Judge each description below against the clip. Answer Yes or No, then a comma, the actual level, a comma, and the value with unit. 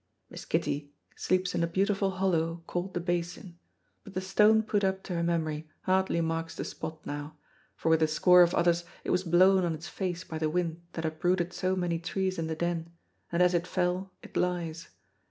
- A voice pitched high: No, medium, 175 Hz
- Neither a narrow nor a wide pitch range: No, narrow, 2.1 semitones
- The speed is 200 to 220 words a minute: Yes, fast, 205 wpm